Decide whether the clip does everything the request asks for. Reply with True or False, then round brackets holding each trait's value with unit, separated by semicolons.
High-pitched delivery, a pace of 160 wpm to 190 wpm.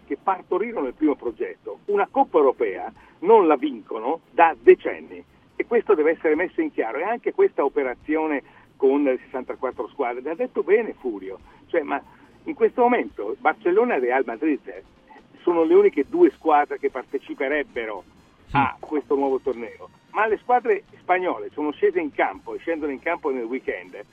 True (375 Hz; 165 wpm)